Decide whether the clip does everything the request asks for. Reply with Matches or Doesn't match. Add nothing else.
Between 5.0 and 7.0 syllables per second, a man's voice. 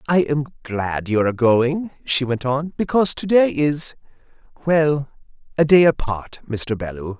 Doesn't match